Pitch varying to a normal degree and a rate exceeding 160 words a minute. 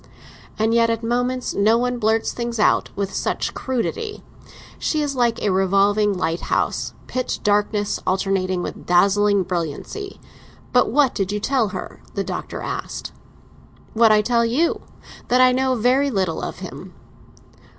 No: average, 4.0 semitones; average, 150 wpm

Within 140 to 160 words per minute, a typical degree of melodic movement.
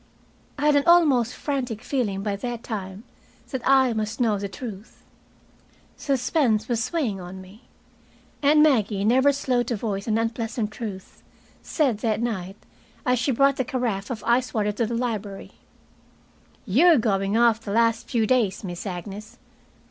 Yes: average, 155 wpm; average, 3.7 semitones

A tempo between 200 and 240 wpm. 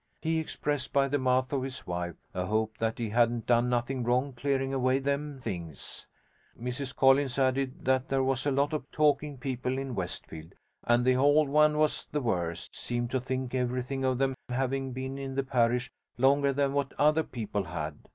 No: average, 190 wpm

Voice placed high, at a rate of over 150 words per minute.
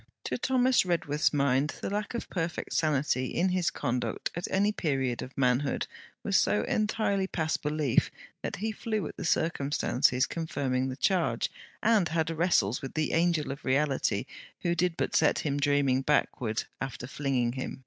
No: medium, 150 Hz; average, 165 wpm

